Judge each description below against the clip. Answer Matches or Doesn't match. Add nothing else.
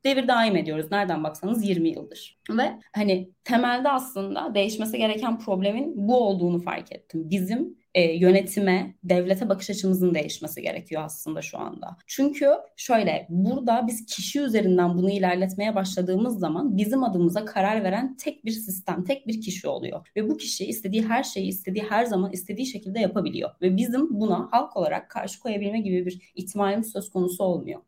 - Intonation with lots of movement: Doesn't match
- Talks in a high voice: Matches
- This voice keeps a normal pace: Doesn't match